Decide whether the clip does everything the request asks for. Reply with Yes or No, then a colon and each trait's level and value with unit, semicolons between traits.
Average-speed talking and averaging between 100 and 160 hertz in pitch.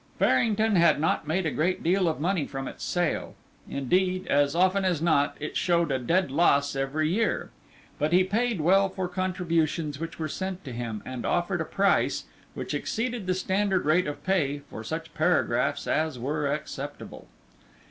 No: average, 175 wpm; medium, 170 Hz